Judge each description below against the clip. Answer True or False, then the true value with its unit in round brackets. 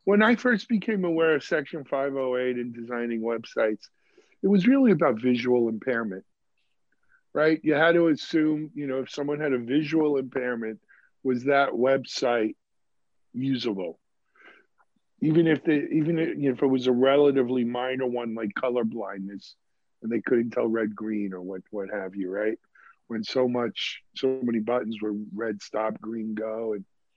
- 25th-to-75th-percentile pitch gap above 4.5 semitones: True (5.1 semitones)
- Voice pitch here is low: True (130 Hz)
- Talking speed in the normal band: True (165 wpm)